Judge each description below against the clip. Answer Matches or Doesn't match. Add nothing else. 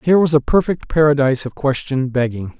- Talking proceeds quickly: Doesn't match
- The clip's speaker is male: Matches